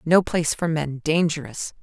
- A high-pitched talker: No, medium, 155 Hz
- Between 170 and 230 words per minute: No, slow, 130 wpm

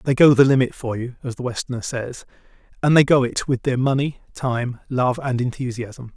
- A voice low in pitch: Yes, low, 125 Hz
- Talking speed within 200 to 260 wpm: Yes, fast, 205 wpm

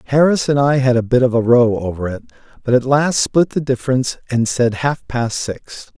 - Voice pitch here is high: No, low, 125 Hz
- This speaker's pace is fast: Yes, fast, 220 wpm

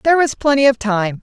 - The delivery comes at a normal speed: No, fast, 245 wpm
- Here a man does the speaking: No, female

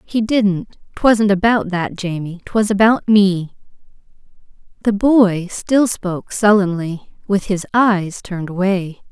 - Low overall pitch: No, high, 195 Hz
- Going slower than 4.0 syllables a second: Yes, 3.8 syllables/s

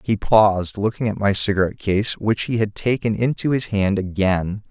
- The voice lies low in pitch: Yes, low, 105 Hz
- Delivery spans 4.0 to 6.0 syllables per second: Yes, 5.0 syllables/s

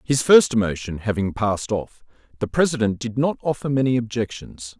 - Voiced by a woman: No, male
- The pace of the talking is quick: No, average, 165 wpm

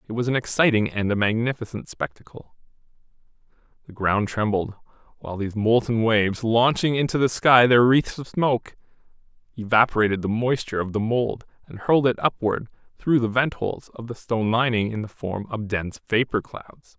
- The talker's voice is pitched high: No, low, 115 Hz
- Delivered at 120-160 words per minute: No, average, 170 wpm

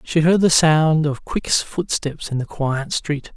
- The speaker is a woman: No, male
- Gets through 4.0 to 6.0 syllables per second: No, 3.7 syllables/s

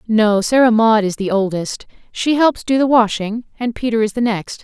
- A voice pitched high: Yes, high, 225 Hz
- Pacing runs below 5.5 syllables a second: Yes, 4.9 syllables/s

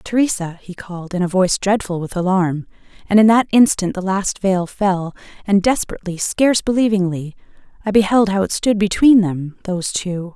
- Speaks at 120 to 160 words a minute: No, average, 170 wpm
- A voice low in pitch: No, high, 195 Hz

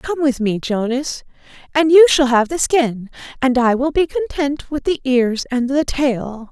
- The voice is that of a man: No, female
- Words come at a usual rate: Yes, average, 195 wpm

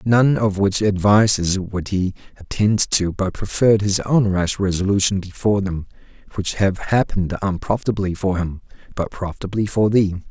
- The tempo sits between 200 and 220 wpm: No, average, 150 wpm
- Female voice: No, male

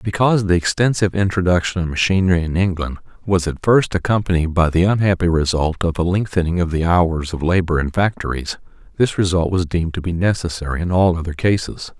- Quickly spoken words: No, average, 185 wpm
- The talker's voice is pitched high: No, very low, 90 Hz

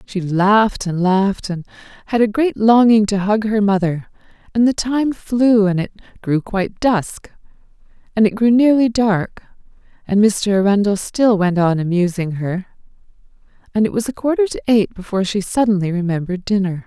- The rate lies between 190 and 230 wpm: No, average, 165 wpm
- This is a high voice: Yes, high, 205 Hz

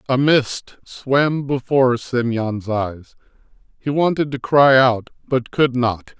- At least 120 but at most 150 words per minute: Yes, slow, 135 wpm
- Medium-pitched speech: No, low, 130 Hz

